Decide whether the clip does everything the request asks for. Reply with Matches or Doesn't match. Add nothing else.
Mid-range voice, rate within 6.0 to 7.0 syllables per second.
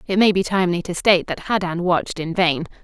Matches